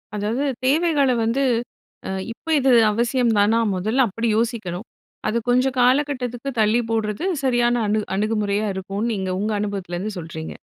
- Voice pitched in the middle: No, high, 225 Hz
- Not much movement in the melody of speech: No, average, 3.4 semitones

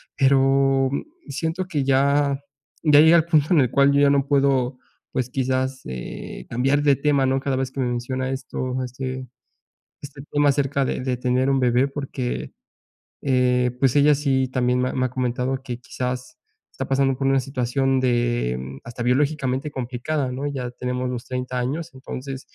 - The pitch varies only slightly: Yes, narrow, 1.7 semitones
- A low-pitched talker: Yes, low, 130 Hz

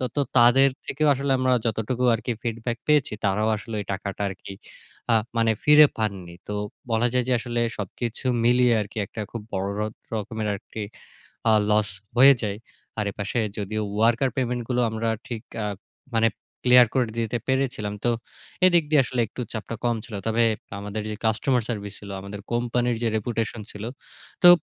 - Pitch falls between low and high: No, low, 115 Hz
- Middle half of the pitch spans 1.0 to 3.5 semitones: Yes, average, 2.7 semitones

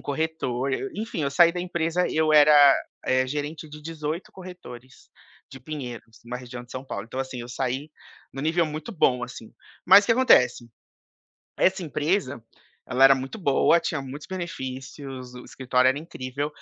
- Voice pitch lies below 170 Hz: Yes, medium, 140 Hz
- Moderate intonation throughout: Yes, average, 4.1 semitones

